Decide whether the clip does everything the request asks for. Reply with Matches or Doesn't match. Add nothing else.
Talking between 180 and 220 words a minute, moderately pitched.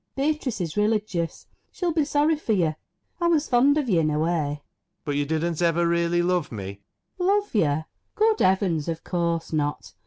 Matches